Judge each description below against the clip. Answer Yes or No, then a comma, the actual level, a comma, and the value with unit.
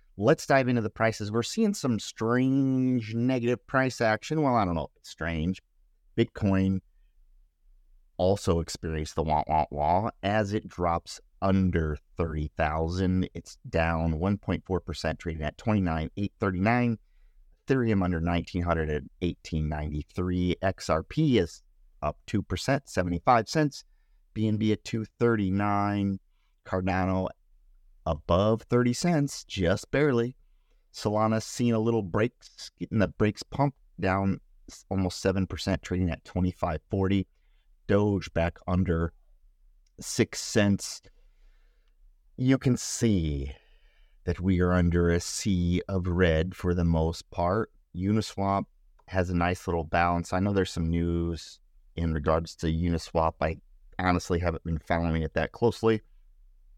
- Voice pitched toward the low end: Yes, very low, 95 Hz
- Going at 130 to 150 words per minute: Yes, slow, 135 wpm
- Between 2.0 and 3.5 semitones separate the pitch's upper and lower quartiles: No, average, 4.5 semitones